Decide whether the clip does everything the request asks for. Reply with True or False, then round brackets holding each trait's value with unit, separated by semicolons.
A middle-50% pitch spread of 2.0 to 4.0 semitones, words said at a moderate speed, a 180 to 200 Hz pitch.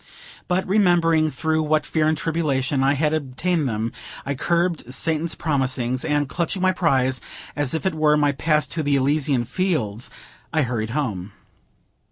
False (3.7 semitones; 160 wpm; 150 Hz)